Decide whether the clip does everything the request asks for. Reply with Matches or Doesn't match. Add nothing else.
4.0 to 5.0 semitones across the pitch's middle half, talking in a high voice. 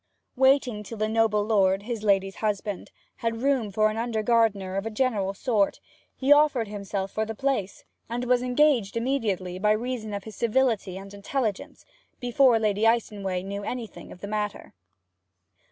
Doesn't match